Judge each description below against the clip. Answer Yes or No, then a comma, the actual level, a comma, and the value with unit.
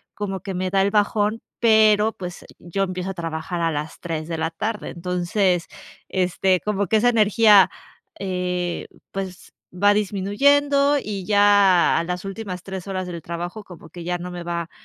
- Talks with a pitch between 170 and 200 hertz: Yes, high, 190 Hz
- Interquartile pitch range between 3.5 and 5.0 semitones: No, average, 2.8 semitones